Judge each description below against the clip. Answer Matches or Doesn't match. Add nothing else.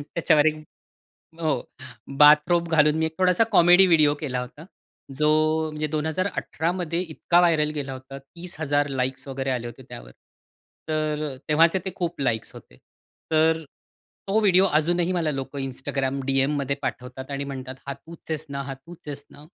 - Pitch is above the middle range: Doesn't match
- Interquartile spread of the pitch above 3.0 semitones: Matches